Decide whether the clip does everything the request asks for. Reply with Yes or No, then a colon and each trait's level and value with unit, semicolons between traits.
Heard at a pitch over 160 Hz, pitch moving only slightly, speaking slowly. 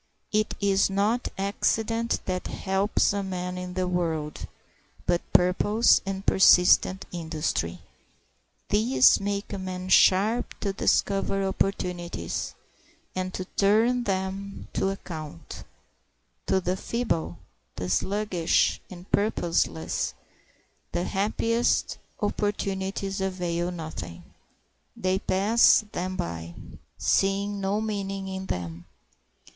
Yes: high, 190 Hz; narrow, 2.2 semitones; slow, 105 wpm